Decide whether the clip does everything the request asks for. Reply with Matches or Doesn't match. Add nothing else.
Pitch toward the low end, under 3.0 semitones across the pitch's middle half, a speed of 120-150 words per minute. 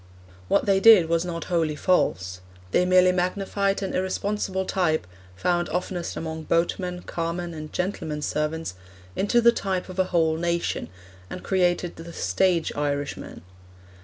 Doesn't match